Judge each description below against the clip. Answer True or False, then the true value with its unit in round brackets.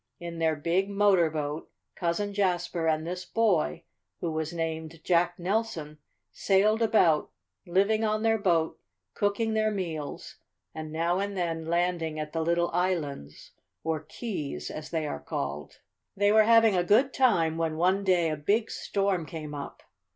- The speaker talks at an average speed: True (160 wpm)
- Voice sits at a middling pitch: True (175 Hz)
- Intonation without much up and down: False (4.1 semitones)